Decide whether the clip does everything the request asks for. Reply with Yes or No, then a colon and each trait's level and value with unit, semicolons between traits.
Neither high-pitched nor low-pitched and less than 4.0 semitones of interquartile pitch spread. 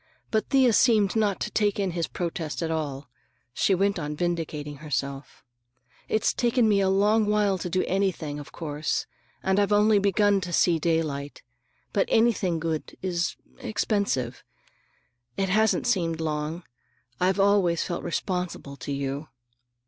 No: medium, 180 Hz; average, 4.7 semitones